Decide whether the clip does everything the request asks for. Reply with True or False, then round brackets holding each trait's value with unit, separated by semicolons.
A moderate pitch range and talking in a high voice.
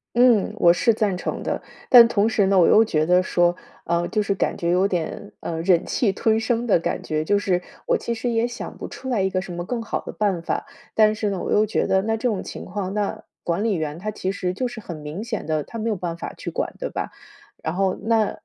True (4.0 semitones; 200 Hz)